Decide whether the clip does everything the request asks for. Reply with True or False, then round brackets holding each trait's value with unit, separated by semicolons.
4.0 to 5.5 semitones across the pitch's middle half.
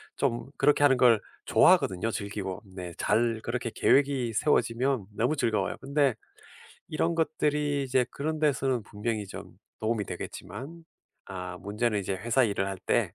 True (5.2 semitones)